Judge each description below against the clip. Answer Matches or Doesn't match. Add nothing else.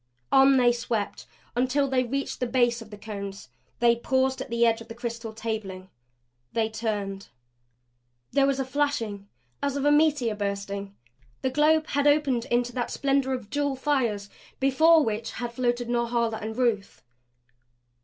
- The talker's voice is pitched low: Doesn't match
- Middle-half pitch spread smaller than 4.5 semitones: Matches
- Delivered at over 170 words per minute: Doesn't match